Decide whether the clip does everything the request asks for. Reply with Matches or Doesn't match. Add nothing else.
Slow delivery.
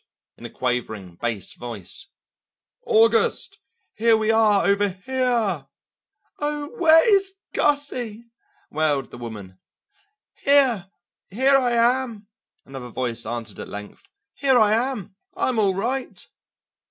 Matches